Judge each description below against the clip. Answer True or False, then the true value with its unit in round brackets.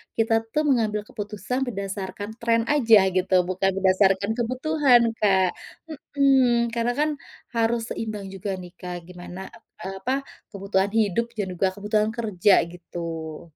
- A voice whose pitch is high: True (210 Hz)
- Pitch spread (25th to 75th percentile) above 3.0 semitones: True (3.7 semitones)